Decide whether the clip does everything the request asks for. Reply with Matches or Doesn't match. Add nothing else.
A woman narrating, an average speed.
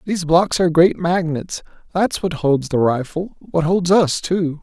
Doesn't match